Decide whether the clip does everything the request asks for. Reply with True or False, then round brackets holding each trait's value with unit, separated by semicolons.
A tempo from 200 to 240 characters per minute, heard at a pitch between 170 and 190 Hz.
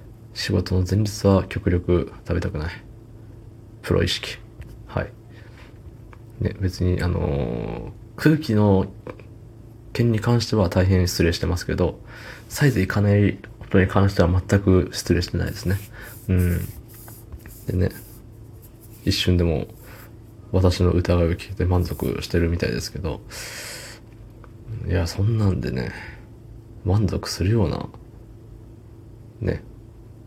False (225 characters per minute; 110 Hz)